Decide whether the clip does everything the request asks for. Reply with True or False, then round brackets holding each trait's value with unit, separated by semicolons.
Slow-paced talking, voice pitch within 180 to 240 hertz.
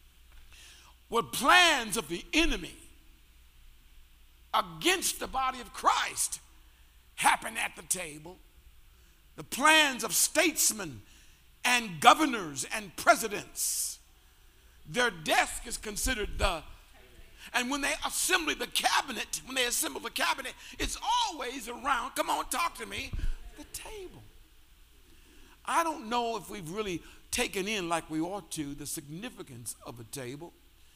True (125 wpm; 190 Hz)